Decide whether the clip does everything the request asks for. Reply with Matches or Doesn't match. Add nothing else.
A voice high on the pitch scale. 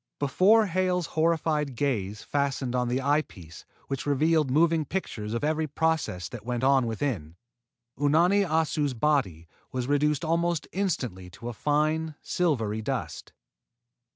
Doesn't match